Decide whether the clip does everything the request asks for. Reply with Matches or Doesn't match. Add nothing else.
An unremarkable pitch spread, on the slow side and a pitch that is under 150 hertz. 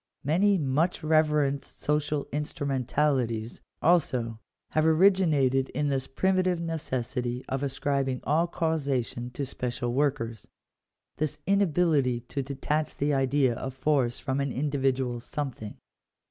Matches